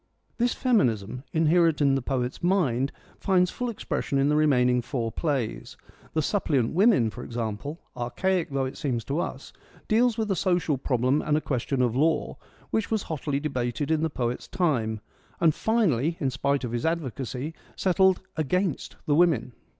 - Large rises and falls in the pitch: Yes, wide, 5.8 semitones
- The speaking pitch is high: No, medium, 145 Hz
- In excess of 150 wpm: Yes, average, 170 wpm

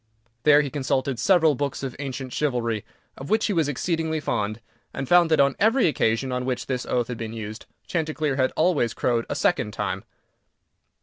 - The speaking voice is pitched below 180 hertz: Yes, low, 135 Hz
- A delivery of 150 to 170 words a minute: No, average, 185 wpm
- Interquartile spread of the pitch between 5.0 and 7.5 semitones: No, average, 4.5 semitones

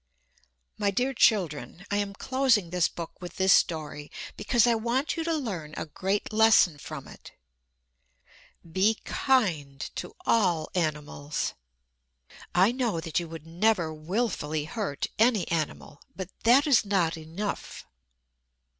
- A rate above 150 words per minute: No, slow, 135 wpm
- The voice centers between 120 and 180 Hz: No, high, 190 Hz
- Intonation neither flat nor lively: No, wide, 5.8 semitones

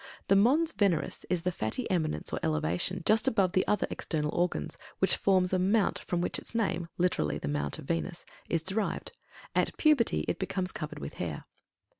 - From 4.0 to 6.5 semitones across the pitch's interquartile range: Yes, average, 4.4 semitones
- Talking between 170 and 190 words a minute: Yes, average, 185 wpm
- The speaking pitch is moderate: Yes, medium, 180 Hz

